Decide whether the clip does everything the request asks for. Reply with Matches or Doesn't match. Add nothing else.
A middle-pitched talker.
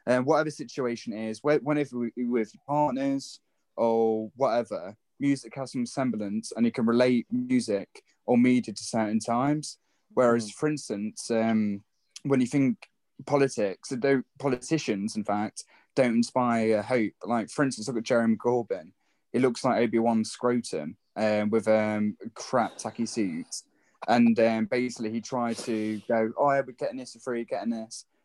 Doesn't match